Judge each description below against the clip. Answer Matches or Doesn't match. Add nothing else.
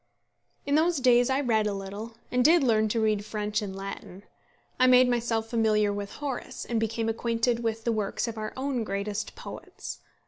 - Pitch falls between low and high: Doesn't match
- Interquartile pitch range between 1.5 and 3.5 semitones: Matches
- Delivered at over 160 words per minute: Matches